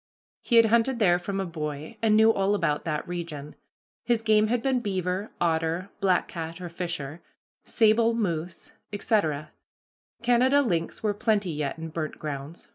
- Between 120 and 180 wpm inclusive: Yes, average, 160 wpm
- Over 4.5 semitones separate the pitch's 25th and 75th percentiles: Yes, average, 5.3 semitones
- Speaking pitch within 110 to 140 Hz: No, medium, 185 Hz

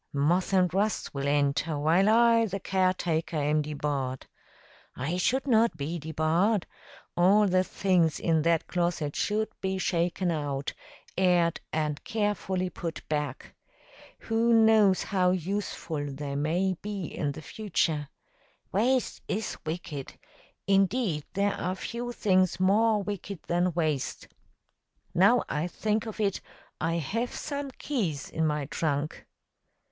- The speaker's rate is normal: No, slow, 130 wpm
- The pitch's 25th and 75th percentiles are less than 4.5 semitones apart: No, average, 4.9 semitones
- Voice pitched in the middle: Yes, medium, 180 Hz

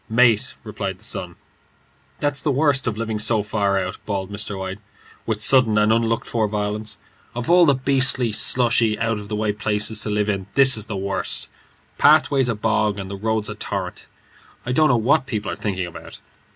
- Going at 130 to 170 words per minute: No, average, 195 wpm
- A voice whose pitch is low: Yes, low, 110 Hz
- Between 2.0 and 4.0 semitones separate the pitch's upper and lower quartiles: Yes, average, 2.9 semitones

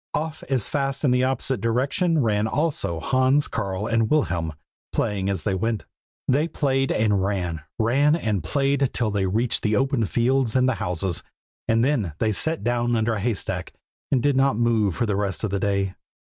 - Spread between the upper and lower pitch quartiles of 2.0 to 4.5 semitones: No, average, 5.1 semitones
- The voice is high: No, low, 115 Hz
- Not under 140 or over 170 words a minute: No, average, 185 wpm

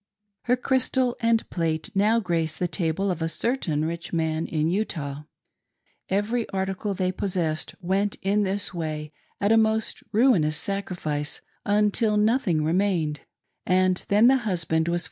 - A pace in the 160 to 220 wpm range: No, average, 145 wpm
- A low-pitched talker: No, medium, 185 Hz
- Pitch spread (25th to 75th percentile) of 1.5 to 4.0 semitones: No, average, 4.6 semitones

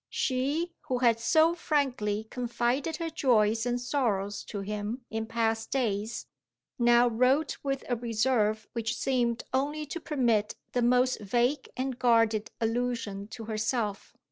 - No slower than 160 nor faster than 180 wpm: No, average, 140 wpm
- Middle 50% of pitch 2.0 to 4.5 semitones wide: Yes, average, 2.9 semitones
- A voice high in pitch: Yes, high, 240 Hz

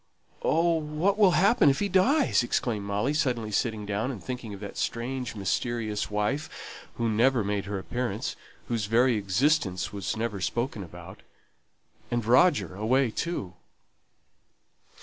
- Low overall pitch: Yes, low, 115 Hz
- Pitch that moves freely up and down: No, average, 5.0 semitones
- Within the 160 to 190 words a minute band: No, average, 140 wpm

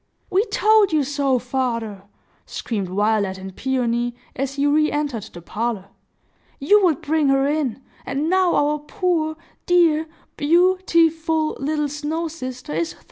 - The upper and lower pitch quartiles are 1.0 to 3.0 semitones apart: No, average, 5.0 semitones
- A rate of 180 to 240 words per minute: No, average, 145 wpm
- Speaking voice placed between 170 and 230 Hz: No, very high, 290 Hz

